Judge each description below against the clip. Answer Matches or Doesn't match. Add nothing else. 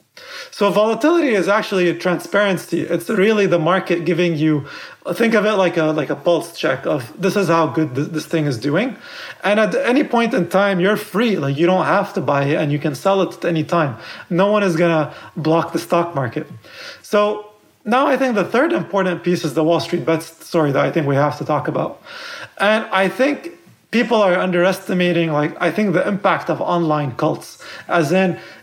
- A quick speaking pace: Matches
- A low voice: Doesn't match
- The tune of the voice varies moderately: Matches